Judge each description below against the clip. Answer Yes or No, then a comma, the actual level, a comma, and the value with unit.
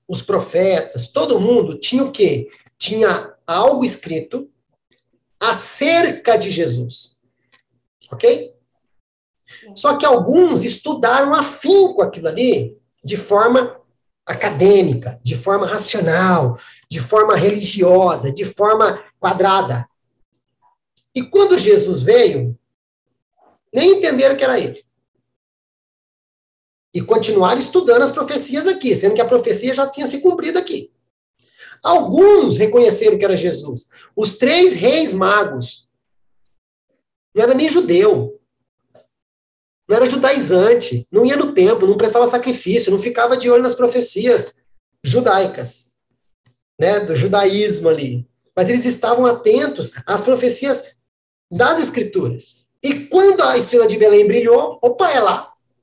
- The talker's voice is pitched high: Yes, high, 240 Hz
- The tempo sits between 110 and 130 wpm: Yes, slow, 120 wpm